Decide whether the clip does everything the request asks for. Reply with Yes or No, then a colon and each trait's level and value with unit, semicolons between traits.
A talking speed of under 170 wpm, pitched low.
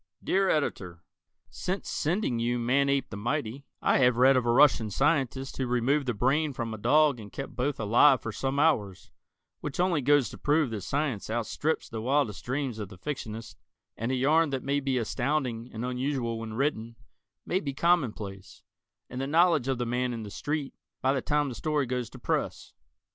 No: average, 195 wpm; low, 130 Hz